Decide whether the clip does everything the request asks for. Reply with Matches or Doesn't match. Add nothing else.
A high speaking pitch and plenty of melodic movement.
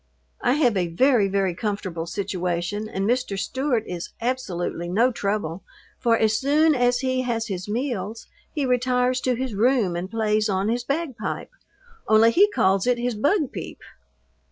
Doesn't match